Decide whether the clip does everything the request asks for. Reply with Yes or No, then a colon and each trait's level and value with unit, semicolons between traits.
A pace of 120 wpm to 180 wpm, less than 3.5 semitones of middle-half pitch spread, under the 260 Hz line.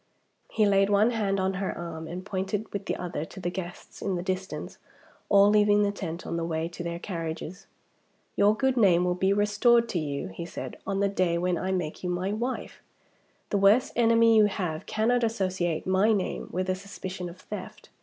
No: fast, 205 wpm; average, 2.8 semitones; high, 190 Hz